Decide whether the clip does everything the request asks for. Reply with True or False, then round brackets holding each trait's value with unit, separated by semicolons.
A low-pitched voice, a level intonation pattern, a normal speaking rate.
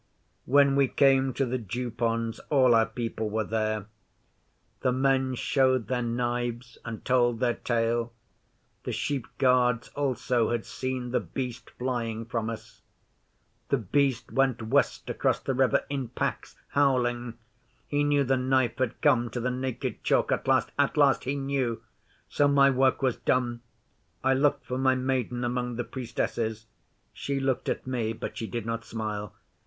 True (125 Hz; 2.3 semitones; 160 wpm)